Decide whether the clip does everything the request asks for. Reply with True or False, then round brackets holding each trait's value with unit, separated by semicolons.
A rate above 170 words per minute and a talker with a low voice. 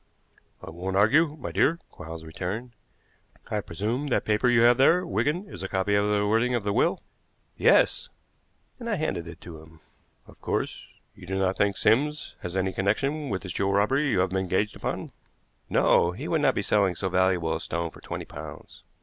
True (200 wpm; 100 Hz)